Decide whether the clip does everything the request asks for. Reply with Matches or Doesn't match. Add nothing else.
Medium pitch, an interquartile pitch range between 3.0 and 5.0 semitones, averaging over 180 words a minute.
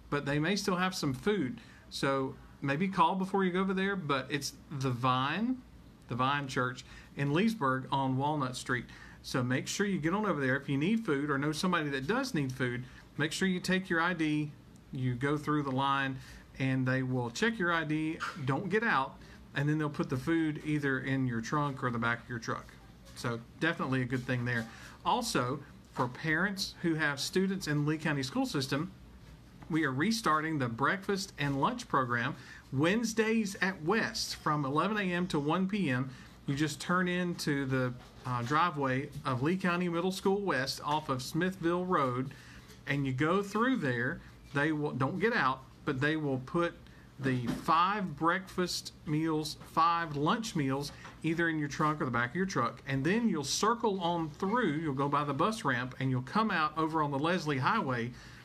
Matches